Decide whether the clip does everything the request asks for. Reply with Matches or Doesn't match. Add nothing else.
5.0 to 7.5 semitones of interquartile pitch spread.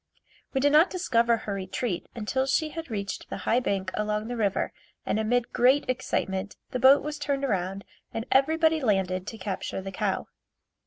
Matches